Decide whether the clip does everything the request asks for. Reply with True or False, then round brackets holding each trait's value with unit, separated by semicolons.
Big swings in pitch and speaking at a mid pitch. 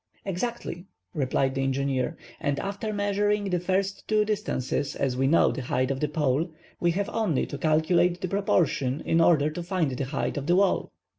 True (6.1 semitones; 165 Hz)